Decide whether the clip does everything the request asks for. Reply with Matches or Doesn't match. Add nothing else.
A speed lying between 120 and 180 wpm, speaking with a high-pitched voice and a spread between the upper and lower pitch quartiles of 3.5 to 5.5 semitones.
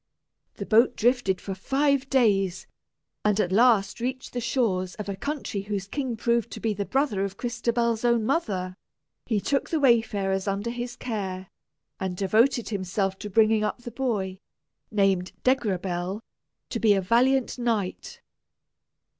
Matches